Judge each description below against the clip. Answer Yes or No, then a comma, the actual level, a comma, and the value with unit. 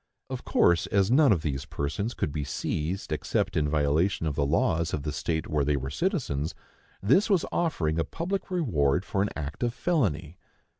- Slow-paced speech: No, average, 190 wpm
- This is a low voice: Yes, very low, 80 Hz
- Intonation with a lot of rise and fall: Yes, wide, 7.8 semitones